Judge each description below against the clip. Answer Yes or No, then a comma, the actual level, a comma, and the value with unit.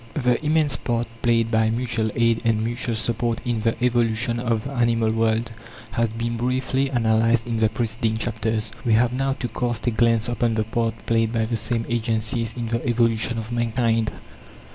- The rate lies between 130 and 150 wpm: No, average, 185 wpm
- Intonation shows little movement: Yes, narrow, 1.2 semitones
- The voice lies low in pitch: Yes, low, 115 Hz